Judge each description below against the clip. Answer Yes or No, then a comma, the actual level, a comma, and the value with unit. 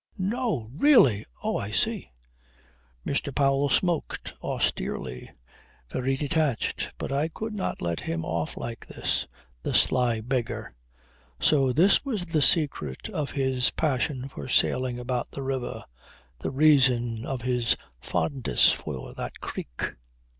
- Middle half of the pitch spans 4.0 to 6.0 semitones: Yes, average, 4.3 semitones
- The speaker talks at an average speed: No, slow, 130 wpm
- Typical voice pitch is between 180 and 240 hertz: No, low, 130 Hz